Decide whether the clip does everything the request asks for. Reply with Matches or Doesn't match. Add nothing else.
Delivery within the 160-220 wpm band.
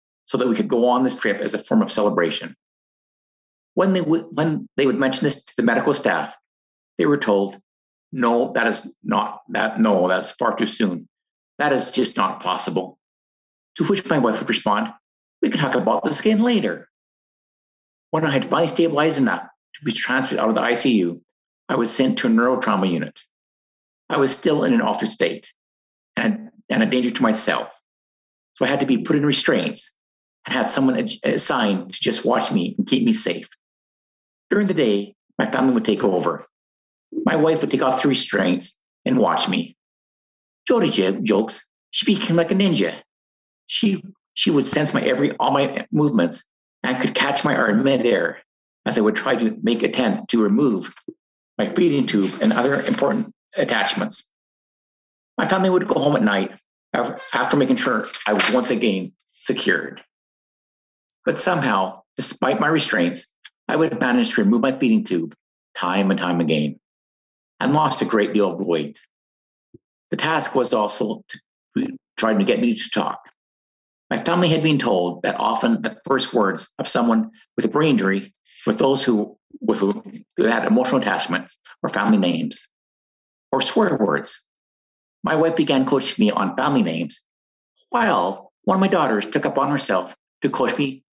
Matches